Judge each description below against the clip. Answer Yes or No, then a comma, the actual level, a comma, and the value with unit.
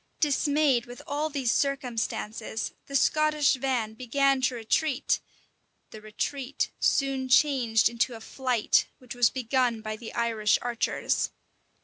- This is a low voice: No, very high, 255 Hz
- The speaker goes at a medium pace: No, slow, 125 wpm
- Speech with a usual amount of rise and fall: Yes, average, 3.2 semitones